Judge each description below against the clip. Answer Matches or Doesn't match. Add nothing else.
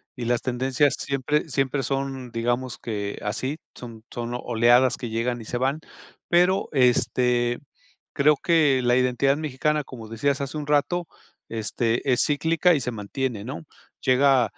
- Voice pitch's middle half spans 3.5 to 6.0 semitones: Doesn't match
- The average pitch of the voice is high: Doesn't match